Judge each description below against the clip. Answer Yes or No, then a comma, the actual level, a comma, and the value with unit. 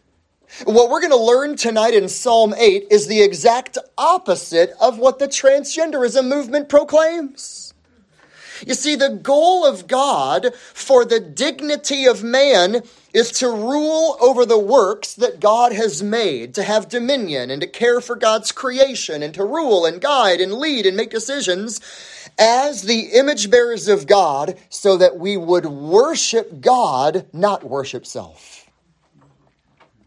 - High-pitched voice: Yes, high, 240 Hz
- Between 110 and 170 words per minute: Yes, average, 150 wpm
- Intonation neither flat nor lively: No, wide, 5.9 semitones